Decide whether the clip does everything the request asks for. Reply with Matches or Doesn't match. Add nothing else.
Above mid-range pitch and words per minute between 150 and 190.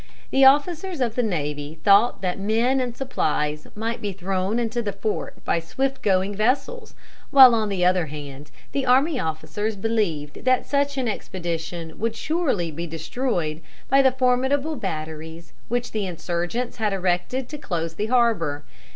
Matches